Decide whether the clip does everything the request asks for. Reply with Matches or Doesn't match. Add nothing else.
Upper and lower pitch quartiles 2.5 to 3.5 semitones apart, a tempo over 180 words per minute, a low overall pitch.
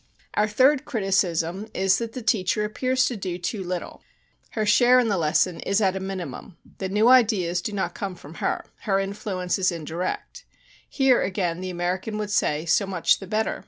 Doesn't match